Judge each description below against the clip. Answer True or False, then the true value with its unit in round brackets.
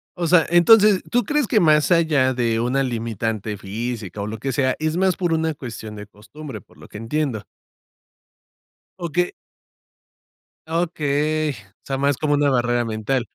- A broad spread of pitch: True (6.1 semitones)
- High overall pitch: False (135 Hz)